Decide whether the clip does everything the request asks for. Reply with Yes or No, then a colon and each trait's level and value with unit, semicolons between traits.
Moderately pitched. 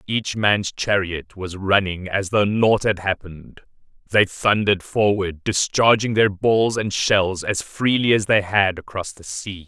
No: low, 100 Hz